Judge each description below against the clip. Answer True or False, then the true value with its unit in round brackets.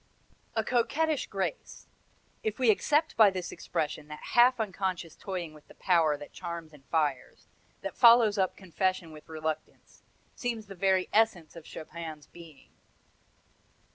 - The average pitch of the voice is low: False (185 Hz)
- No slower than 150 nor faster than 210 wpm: False (140 wpm)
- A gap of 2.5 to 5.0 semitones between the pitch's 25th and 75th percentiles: False (5.6 semitones)